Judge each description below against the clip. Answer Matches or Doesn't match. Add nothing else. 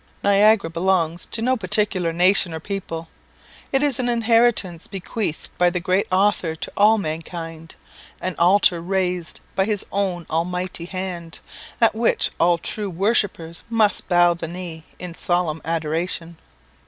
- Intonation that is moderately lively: Matches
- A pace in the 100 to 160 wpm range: Matches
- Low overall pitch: Doesn't match